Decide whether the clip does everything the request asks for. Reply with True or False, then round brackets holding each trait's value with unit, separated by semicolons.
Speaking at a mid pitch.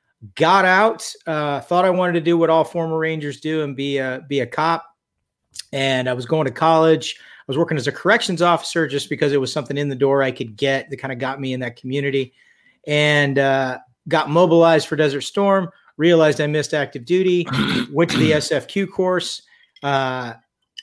True (150 Hz)